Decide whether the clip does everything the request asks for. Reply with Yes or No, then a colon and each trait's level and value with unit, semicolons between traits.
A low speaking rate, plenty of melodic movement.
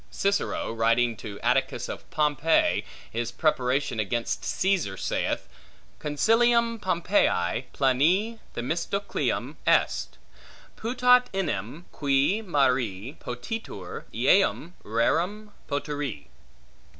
Yes: slow, 85 wpm; wide, 8.7 semitones